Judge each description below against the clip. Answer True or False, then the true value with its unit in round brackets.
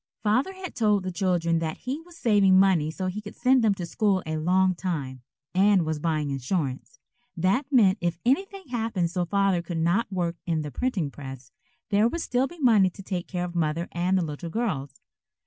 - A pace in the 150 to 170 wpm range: False (200 wpm)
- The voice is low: False (185 Hz)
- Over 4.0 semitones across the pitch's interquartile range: True (4.7 semitones)